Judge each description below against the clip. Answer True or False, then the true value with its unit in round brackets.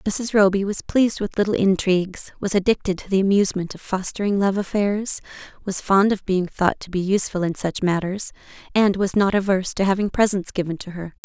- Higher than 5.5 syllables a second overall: True (5.7 syllables/s)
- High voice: True (195 Hz)